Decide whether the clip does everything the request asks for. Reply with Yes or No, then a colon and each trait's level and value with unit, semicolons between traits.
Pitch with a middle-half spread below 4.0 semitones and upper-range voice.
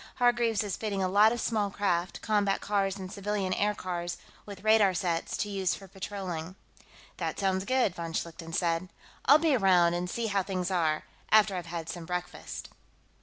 Yes: average, 2.9 semitones; high, 195 Hz